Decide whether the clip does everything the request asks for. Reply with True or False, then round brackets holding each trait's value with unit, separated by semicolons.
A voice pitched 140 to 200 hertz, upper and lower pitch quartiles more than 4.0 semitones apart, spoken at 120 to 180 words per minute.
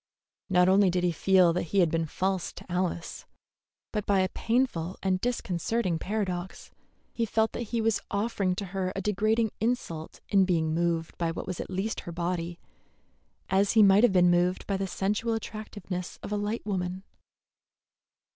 False (190 Hz; 2.9 semitones; 175 wpm)